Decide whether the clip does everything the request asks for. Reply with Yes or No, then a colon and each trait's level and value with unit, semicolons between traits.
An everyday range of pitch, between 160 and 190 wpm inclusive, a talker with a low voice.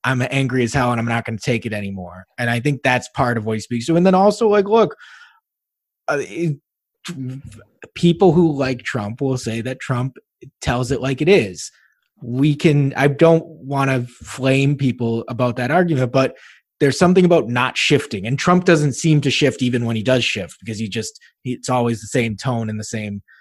No: average, 3.9 semitones; fast, 205 wpm; low, 130 Hz